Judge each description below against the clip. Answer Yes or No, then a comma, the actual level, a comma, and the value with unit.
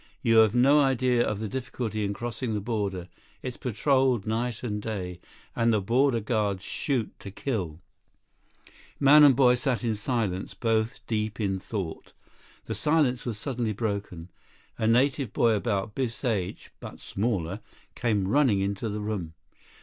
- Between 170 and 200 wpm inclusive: No, average, 155 wpm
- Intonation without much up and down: No, average, 3.5 semitones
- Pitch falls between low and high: No, low, 110 Hz